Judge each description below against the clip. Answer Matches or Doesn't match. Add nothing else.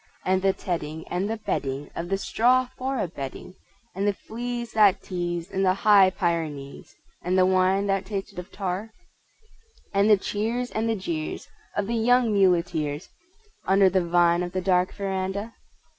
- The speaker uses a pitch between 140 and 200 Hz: Matches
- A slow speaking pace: Doesn't match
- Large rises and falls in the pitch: Doesn't match